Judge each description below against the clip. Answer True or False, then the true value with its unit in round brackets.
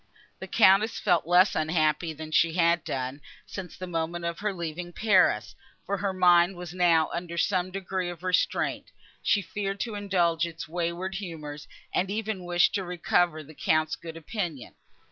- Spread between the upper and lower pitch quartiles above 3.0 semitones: False (2.5 semitones)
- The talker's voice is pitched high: False (175 Hz)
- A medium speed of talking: True (165 wpm)